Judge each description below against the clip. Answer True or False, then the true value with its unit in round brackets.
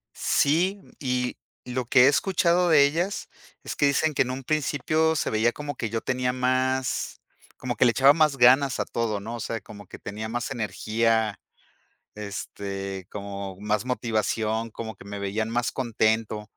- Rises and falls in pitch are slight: False (4.1 semitones)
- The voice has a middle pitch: False (120 Hz)